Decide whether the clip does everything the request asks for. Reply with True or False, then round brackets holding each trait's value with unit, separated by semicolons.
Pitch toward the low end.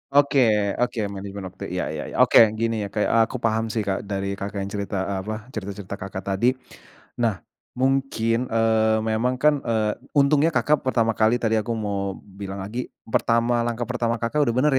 True (110 Hz)